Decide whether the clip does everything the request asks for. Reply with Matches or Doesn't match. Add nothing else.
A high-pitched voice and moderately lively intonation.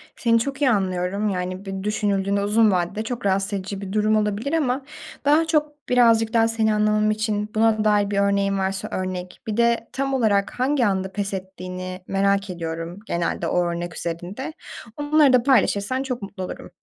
Matches